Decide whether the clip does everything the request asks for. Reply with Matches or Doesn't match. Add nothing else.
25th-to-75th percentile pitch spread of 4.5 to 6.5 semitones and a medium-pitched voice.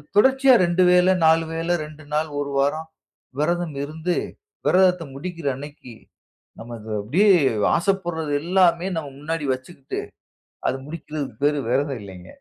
Doesn't match